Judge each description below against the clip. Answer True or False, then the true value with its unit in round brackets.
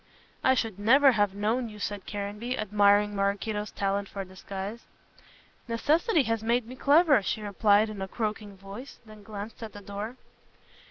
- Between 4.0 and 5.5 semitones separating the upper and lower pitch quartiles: False (2.4 semitones)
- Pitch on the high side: True (210 Hz)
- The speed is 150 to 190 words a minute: True (160 wpm)